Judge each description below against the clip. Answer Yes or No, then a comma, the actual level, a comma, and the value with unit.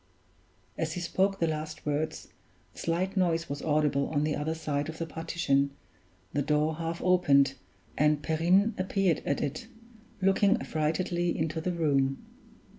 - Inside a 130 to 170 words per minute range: Yes, average, 150 wpm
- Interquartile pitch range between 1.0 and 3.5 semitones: Yes, average, 2.7 semitones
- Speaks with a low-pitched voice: No, medium, 160 Hz